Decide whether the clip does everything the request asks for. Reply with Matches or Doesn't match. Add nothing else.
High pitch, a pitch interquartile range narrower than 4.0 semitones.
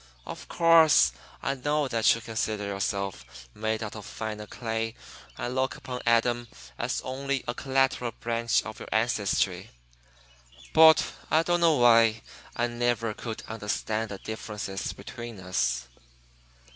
Doesn't match